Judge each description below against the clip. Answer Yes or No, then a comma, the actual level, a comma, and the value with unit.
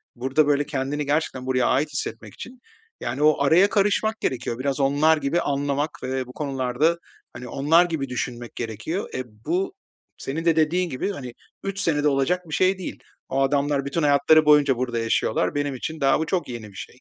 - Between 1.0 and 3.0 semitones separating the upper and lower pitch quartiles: No, average, 3.5 semitones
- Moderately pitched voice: Yes, medium, 145 Hz